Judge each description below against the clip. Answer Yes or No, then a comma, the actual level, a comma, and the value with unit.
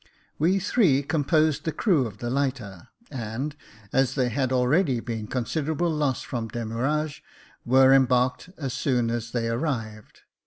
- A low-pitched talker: Yes, low, 130 Hz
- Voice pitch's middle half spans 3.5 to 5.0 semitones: Yes, average, 4.2 semitones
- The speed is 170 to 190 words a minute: No, average, 150 wpm